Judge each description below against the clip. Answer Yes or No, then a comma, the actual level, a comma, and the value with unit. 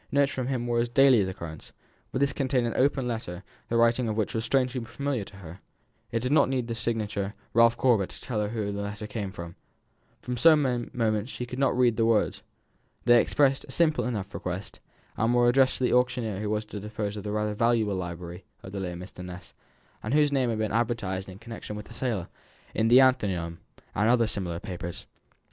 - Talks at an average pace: No, fast, 215 wpm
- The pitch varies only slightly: No, average, 3.7 semitones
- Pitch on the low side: Yes, low, 115 Hz